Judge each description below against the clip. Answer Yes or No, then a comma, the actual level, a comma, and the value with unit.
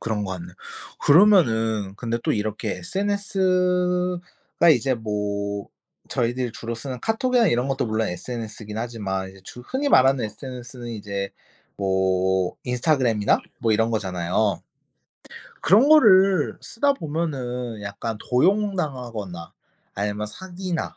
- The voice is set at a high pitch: No, low, 120 Hz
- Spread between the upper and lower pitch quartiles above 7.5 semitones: Yes, wide, 9.0 semitones